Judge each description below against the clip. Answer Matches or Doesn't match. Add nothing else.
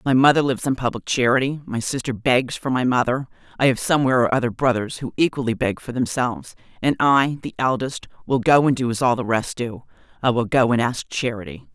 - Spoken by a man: Doesn't match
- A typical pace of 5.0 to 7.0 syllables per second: Matches